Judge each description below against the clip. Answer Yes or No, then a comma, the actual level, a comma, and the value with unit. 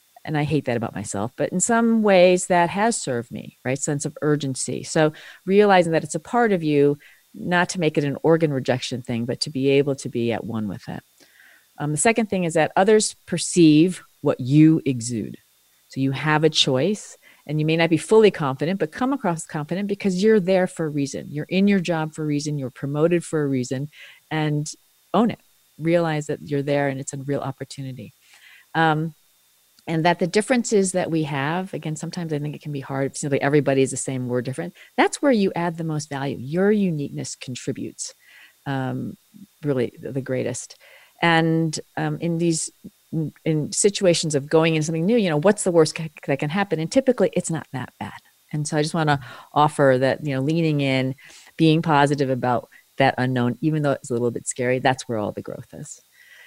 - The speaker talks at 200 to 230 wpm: Yes, fast, 205 wpm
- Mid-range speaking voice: Yes, medium, 155 Hz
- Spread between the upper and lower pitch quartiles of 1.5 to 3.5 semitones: No, average, 4.4 semitones